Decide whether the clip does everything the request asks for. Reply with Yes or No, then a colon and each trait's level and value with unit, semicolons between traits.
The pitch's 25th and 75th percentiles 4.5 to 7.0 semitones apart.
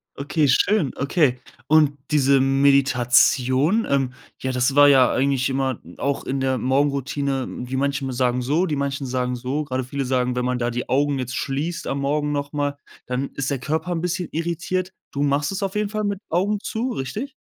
No: average, 2.7 semitones